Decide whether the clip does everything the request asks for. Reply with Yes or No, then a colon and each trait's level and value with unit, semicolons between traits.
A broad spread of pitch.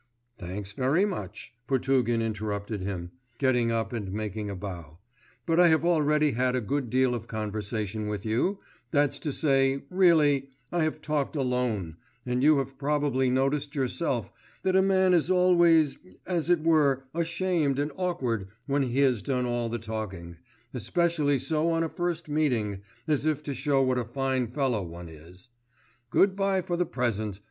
Yes: wide, 5.8 semitones